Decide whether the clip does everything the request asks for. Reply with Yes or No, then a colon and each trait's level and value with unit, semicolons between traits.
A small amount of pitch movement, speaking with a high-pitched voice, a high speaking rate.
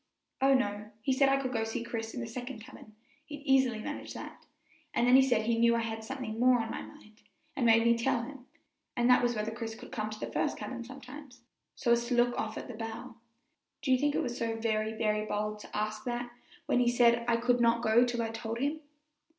Yes: narrow, 2.1 semitones; high, 235 Hz; fast, 245 wpm